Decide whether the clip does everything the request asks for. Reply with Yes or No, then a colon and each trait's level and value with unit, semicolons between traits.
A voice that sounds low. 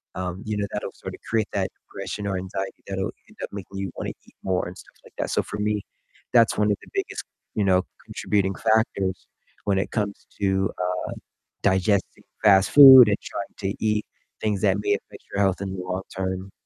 Yes: low, 100 Hz